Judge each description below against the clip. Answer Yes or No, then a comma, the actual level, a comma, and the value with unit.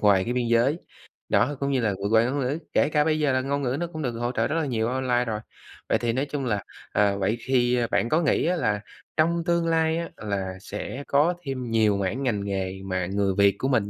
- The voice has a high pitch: No, low, 125 Hz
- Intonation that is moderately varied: No, wide, 5.7 semitones